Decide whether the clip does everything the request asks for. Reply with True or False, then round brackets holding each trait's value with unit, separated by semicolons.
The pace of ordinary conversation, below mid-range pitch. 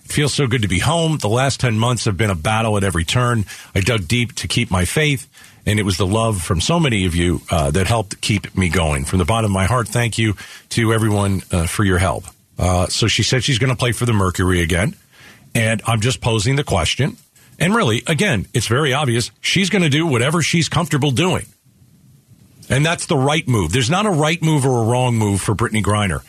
False (235 wpm; 115 Hz)